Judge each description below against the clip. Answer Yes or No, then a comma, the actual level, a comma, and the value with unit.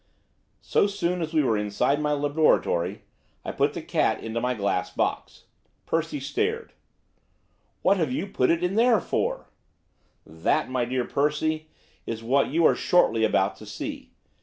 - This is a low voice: No, medium, 145 Hz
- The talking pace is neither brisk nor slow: Yes, average, 155 wpm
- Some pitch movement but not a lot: No, wide, 6.4 semitones